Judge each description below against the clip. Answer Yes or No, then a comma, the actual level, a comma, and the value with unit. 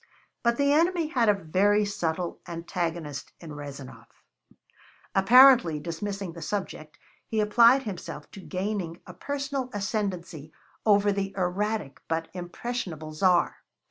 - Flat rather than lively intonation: No, average, 4.7 semitones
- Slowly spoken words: Yes, slow, 120 wpm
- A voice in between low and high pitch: No, high, 195 Hz